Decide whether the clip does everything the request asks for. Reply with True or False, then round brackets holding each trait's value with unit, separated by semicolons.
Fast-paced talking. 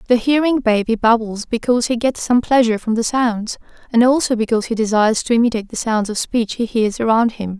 True (215 wpm)